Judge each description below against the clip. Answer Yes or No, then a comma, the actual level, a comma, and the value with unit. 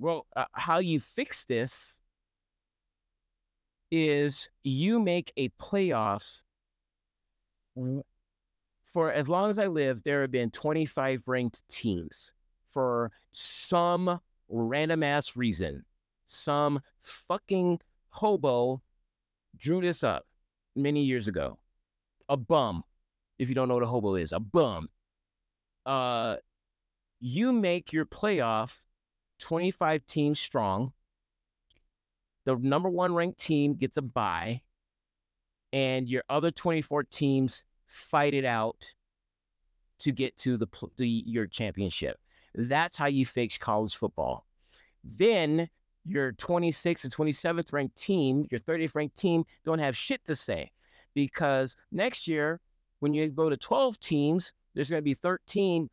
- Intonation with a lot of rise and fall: Yes, wide, 6.3 semitones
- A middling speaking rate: No, slow, 125 wpm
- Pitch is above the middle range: No, low, 135 Hz